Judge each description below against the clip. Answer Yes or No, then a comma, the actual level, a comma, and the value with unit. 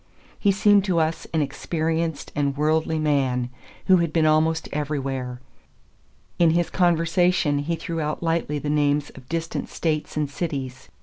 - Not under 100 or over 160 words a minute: Yes, average, 150 wpm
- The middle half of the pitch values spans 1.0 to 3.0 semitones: Yes, narrow, 2.6 semitones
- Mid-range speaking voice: Yes, medium, 155 Hz